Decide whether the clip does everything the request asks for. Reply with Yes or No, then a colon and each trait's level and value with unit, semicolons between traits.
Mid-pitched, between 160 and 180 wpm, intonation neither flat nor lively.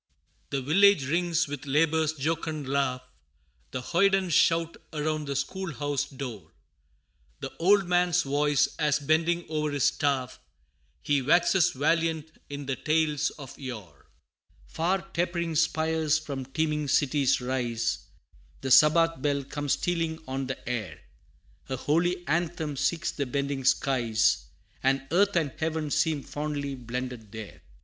No: medium, 150 Hz; slow, 135 wpm; average, 3.5 semitones